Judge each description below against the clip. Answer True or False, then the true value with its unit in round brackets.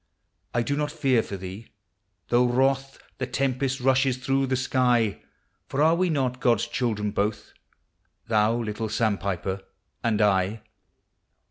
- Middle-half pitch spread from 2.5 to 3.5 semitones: False (4.0 semitones)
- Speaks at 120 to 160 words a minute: True (140 wpm)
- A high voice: False (120 Hz)